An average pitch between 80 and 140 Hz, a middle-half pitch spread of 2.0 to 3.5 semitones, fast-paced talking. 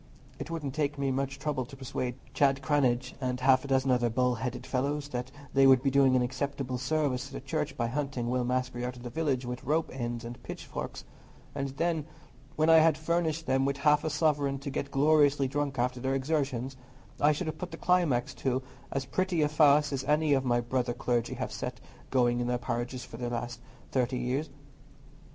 Yes: low, 135 Hz; average, 2.8 semitones; fast, 210 wpm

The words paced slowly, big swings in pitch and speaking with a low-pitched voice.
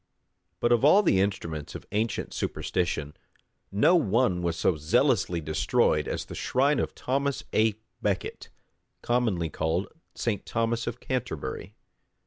Yes: slow, 130 wpm; wide, 6.5 semitones; low, 105 Hz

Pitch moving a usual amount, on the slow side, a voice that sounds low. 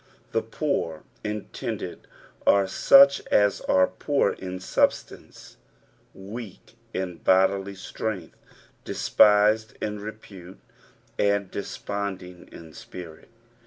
No: narrow, 2.2 semitones; slow, 90 wpm; low, 100 Hz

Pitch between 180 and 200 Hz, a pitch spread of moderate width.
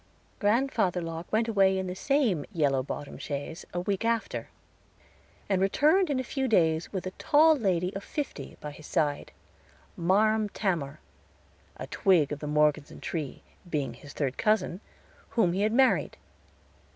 No: medium, 185 Hz; wide, 6.1 semitones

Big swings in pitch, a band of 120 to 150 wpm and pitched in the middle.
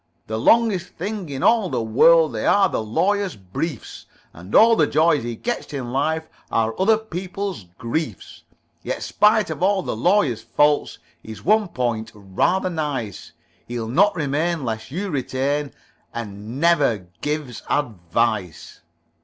Yes: wide, 8.1 semitones; average, 145 wpm; medium, 145 Hz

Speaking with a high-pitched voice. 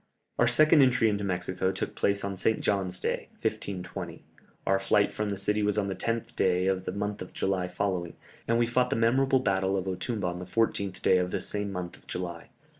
No: low, 100 Hz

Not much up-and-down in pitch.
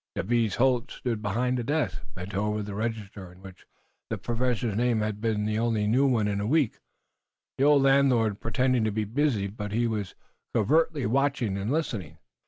No: average, 3.5 semitones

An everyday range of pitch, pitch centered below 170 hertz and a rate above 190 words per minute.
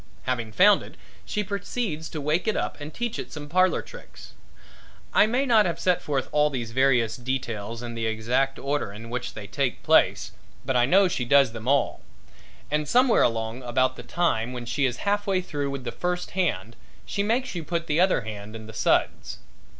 No: wide, 7.3 semitones; medium, 140 Hz; fast, 205 wpm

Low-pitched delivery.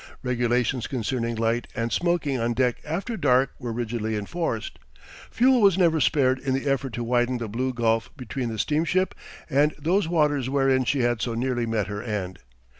Yes: low, 125 Hz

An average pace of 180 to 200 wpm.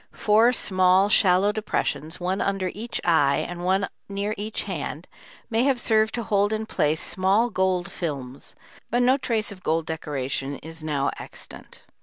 No: average, 160 wpm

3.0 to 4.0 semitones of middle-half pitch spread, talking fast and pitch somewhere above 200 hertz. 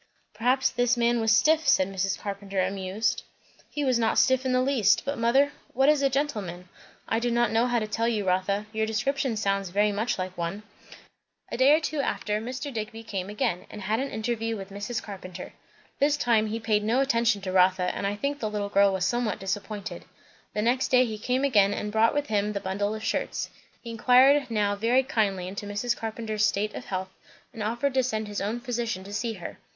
Yes: average, 3.5 semitones; fast, 215 wpm; high, 220 Hz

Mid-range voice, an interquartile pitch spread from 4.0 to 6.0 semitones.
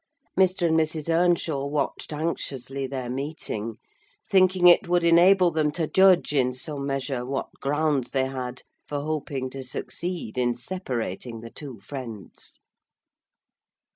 Yes: medium, 145 Hz; average, 4.6 semitones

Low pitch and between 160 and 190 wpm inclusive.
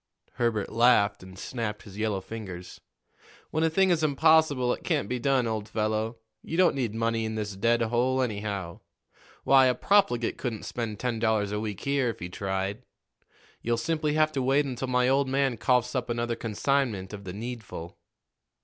Yes: low, 115 Hz; average, 180 wpm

